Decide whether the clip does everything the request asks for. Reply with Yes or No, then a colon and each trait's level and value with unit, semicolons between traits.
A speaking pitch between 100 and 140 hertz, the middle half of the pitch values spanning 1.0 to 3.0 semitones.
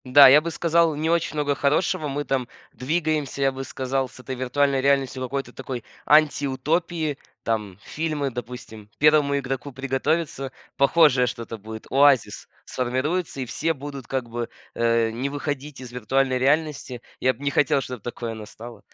Yes: low, 135 Hz; average, 2.7 semitones